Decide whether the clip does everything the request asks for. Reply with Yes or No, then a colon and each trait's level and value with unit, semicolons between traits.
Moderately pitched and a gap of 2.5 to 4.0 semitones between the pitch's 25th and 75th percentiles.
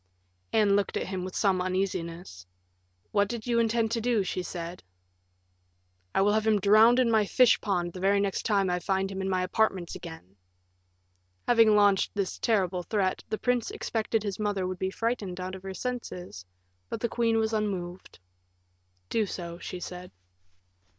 No: high, 195 Hz; average, 3.2 semitones